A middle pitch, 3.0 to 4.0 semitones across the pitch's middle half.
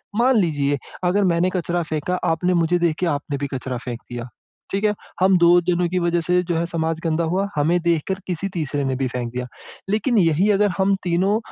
Yes: medium, 170 Hz; average, 3.6 semitones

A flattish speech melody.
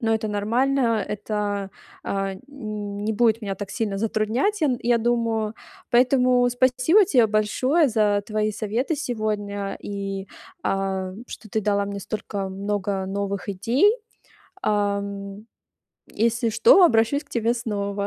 No: average, 3.0 semitones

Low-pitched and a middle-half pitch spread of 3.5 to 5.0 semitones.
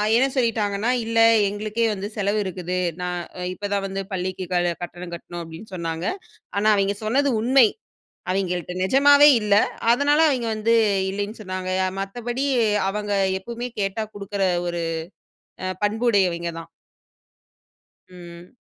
No: high, 200 Hz; average, 4.0 semitones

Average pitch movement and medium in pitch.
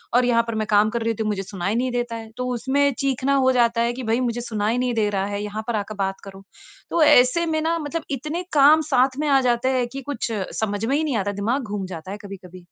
No: average, 4.1 semitones; high, 235 Hz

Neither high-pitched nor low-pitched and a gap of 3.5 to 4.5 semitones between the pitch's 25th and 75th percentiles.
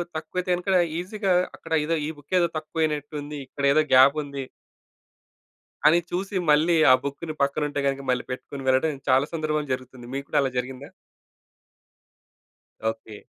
No: medium, 145 Hz; average, 3.0 semitones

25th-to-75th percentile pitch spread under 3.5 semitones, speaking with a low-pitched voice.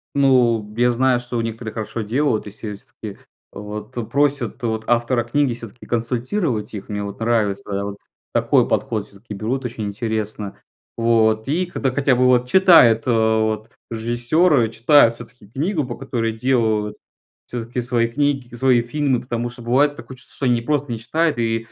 Yes: average, 2.8 semitones; low, 120 Hz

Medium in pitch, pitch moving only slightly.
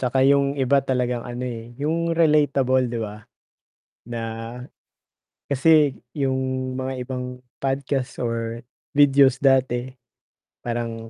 No: low, 130 Hz; narrow, 2.3 semitones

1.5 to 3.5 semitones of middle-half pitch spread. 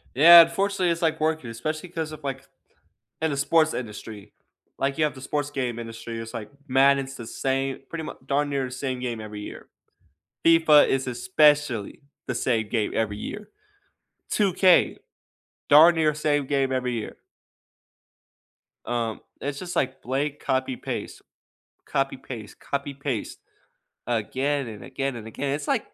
No: average, 3.9 semitones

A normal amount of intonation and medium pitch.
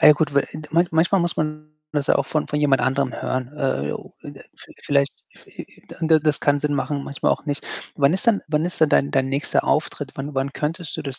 No: narrow, 2.2 semitones; medium, 150 Hz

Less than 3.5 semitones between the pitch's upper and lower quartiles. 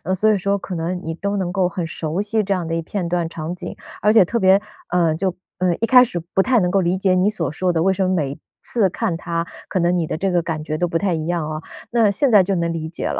Yes: average, 2.9 semitones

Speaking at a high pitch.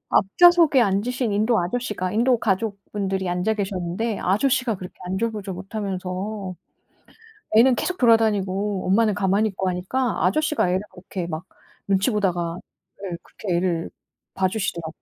Yes: high, 200 Hz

